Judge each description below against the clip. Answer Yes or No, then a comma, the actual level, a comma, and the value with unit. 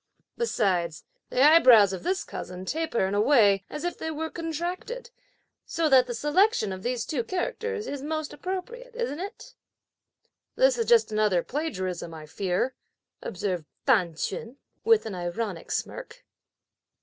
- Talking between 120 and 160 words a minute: Yes, average, 150 wpm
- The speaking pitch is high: Yes, very high, 270 Hz